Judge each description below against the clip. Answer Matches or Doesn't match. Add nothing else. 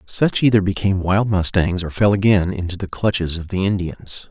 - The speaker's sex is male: Matches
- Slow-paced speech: Doesn't match